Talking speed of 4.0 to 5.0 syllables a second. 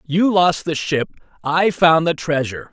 Yes: 4.5 syllables/s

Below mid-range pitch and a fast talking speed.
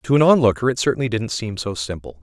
Yes: low, 115 Hz; fast, 240 wpm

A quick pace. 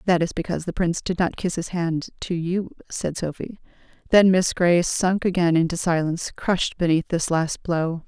No: average, 195 wpm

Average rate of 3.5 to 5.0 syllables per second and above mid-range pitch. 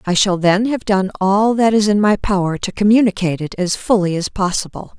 No: 5.3 syllables/s; high, 200 Hz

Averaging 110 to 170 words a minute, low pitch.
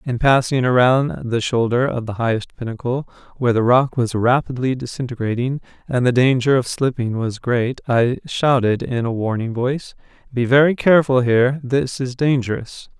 Yes: average, 160 wpm; low, 125 Hz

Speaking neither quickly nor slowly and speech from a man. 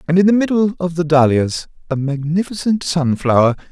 Yes: average, 160 wpm; male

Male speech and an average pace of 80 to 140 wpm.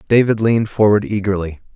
Yes: male; slow, 135 wpm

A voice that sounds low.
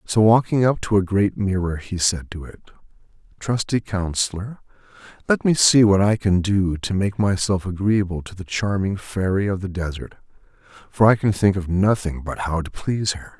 Yes: low, 100 Hz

